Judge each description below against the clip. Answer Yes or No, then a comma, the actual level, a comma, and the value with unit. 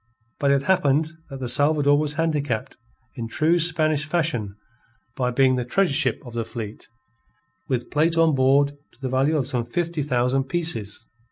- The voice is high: No, medium, 140 Hz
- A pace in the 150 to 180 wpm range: Yes, average, 170 wpm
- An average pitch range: Yes, average, 3.8 semitones